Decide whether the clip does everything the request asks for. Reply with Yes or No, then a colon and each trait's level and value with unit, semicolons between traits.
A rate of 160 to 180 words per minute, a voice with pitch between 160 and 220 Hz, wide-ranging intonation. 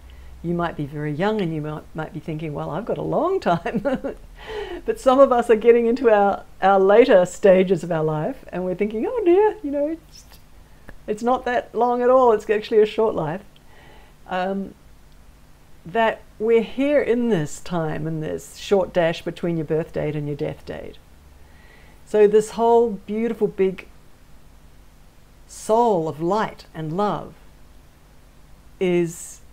Yes: average, 165 wpm; high, 190 Hz; wide, 6.7 semitones